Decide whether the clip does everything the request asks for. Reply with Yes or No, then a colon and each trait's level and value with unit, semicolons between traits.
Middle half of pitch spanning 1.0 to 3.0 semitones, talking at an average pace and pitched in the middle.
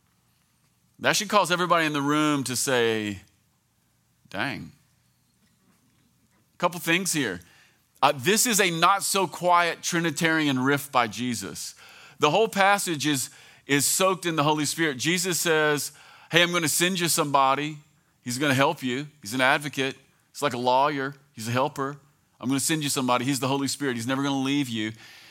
No: average, 3.9 semitones; average, 180 wpm; medium, 145 Hz